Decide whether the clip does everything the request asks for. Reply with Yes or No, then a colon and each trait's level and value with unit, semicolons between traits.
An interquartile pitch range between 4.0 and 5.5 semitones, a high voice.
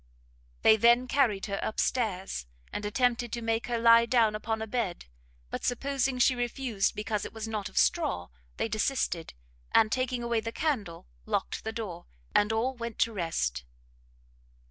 No: average, 2.7 semitones; high, 225 Hz